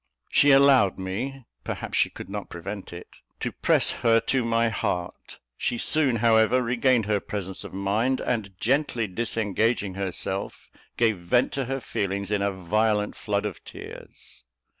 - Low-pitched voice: Yes, low, 110 Hz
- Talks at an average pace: Yes, average, 155 wpm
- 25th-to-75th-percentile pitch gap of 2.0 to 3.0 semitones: No, average, 3.6 semitones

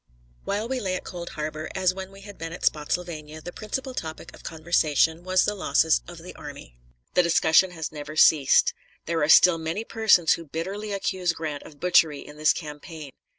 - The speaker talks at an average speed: Yes, average, 195 wpm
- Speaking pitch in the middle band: Yes, medium, 165 Hz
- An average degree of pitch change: Yes, average, 3.3 semitones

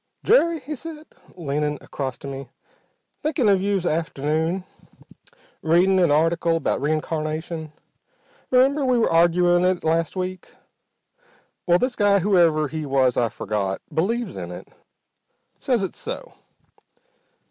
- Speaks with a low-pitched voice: No, medium, 170 Hz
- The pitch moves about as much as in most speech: Yes, average, 4.8 semitones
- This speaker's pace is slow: Yes, slow, 125 wpm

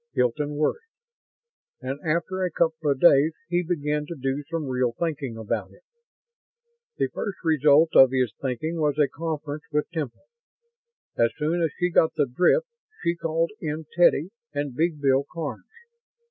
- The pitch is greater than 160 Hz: No, medium, 150 Hz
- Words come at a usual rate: Yes, average, 160 wpm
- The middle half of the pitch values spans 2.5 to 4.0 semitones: Yes, average, 3.2 semitones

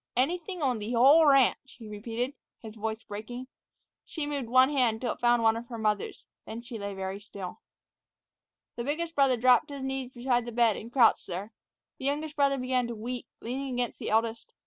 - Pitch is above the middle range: Yes, high, 245 Hz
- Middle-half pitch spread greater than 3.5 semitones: No, average, 3.2 semitones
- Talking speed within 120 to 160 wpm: No, average, 200 wpm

